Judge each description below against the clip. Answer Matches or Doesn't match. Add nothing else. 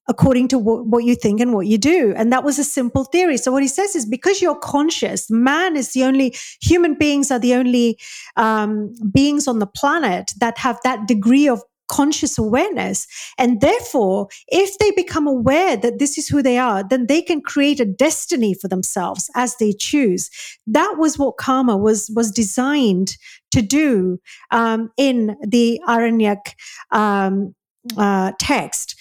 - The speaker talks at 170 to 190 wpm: Matches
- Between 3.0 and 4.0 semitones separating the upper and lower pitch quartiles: Doesn't match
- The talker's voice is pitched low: Doesn't match